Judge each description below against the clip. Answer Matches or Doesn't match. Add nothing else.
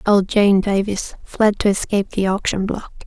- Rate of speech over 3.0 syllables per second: Matches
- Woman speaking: Matches